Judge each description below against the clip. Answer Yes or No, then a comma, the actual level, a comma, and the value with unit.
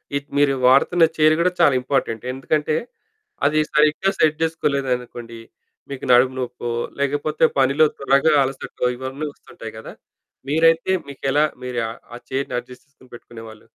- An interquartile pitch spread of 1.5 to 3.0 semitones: No, average, 3.4 semitones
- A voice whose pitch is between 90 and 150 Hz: Yes, medium, 140 Hz